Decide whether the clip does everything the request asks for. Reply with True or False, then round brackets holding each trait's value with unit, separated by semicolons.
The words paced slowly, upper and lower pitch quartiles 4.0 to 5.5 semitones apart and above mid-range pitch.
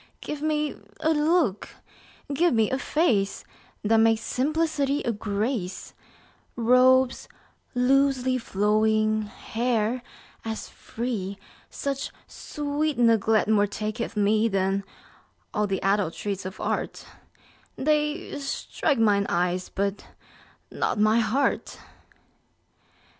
True (105 wpm; 4.8 semitones; 225 Hz)